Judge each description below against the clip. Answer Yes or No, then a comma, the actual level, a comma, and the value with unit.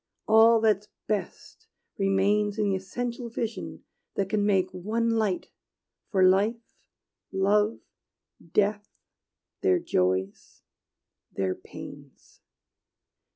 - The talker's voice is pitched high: Yes, high, 205 Hz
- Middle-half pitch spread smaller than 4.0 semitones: Yes, average, 2.7 semitones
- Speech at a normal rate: No, slow, 95 wpm